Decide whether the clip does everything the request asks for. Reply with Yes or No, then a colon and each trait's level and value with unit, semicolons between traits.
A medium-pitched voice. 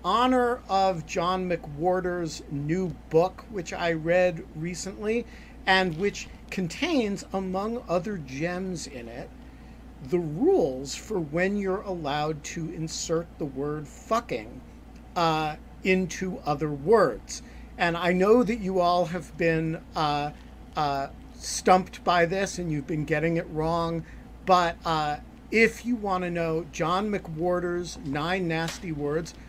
Yes: medium, 175 Hz